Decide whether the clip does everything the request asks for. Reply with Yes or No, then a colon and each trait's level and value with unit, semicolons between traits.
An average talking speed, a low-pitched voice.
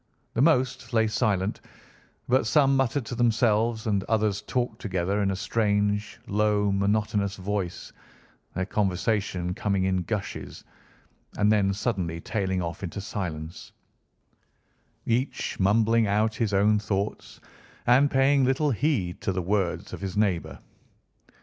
No: slow, 130 wpm; low, 105 Hz